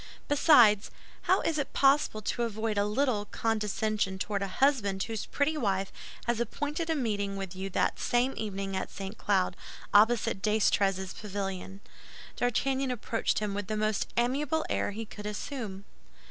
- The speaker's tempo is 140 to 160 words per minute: Yes, average, 155 wpm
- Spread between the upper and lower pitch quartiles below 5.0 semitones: Yes, average, 3.7 semitones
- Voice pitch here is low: No, high, 215 Hz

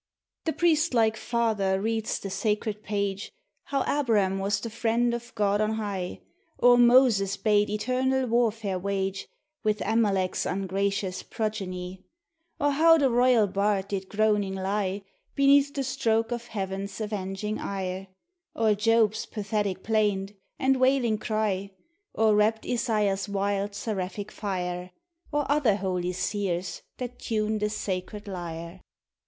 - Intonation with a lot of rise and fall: No, average, 3.0 semitones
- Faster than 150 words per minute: No, slow, 135 wpm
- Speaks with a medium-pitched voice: No, high, 210 Hz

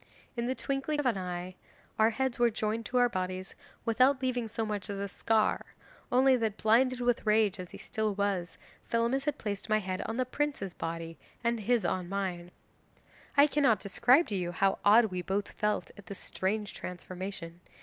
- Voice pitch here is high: Yes, high, 215 Hz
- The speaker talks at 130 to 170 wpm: No, average, 190 wpm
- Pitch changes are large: No, average, 4.4 semitones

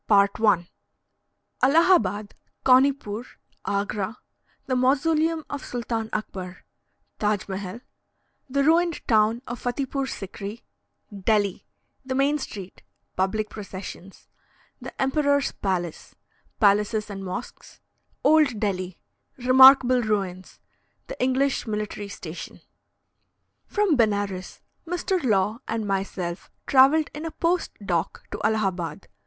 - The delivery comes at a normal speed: No, slow, 100 wpm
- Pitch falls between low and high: No, high, 220 Hz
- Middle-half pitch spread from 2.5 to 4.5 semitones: No, wide, 5.5 semitones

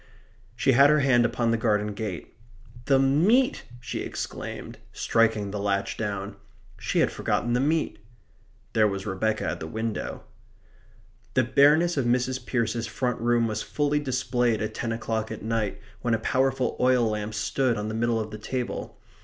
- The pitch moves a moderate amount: Yes, average, 3.2 semitones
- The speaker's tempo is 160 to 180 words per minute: Yes, average, 170 wpm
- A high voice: No, low, 115 Hz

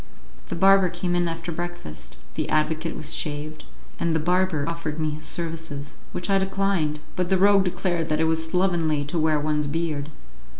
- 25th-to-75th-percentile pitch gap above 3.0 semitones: No, narrow, 2.5 semitones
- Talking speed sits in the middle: Yes, average, 180 wpm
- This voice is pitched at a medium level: Yes, medium, 165 Hz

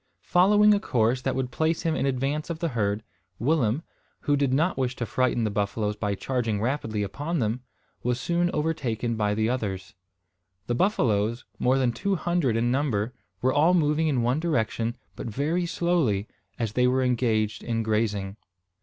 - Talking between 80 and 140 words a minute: No, average, 175 wpm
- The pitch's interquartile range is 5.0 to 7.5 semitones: Yes, wide, 5.6 semitones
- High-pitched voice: No, low, 125 Hz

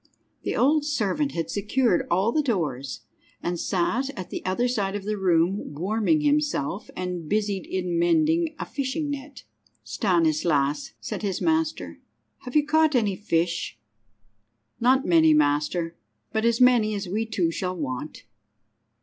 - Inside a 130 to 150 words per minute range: Yes, average, 145 wpm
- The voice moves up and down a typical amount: No, wide, 7.4 semitones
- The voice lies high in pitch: Yes, high, 200 Hz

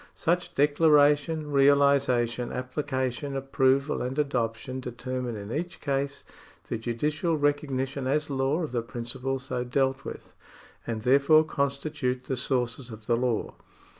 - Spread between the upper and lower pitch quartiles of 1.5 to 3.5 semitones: Yes, narrow, 2.5 semitones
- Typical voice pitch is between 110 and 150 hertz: Yes, low, 135 Hz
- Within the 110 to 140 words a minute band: Yes, slow, 135 wpm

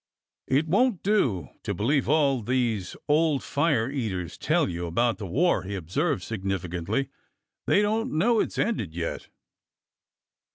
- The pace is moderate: Yes, average, 150 wpm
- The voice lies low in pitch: Yes, low, 130 Hz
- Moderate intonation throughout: No, wide, 8.6 semitones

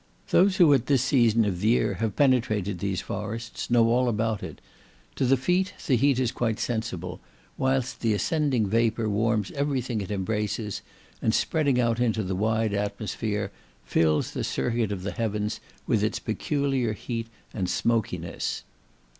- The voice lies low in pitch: Yes, low, 115 Hz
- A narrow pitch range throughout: No, average, 3.4 semitones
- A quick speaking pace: No, average, 165 wpm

